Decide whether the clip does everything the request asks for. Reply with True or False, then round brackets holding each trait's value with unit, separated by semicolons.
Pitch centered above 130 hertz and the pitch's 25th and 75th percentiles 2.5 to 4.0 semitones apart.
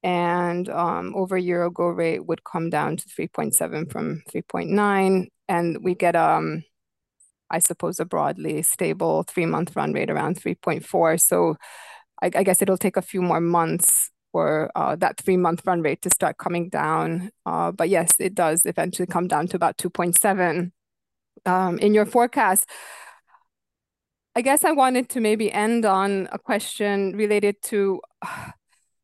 True (185 Hz; 3.1 semitones)